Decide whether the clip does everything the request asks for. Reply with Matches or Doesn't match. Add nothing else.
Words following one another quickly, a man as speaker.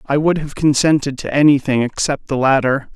Doesn't match